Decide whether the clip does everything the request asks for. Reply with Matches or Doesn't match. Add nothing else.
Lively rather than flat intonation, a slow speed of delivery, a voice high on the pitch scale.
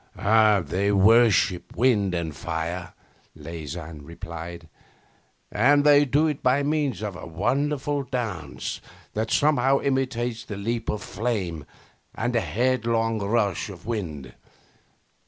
Doesn't match